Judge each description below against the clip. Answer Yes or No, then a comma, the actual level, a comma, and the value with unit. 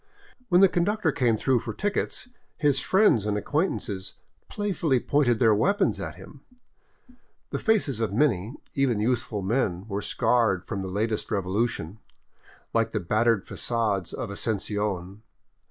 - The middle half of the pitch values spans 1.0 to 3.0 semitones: No, average, 5.2 semitones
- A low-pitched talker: Yes, low, 115 Hz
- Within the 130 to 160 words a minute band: Yes, average, 150 wpm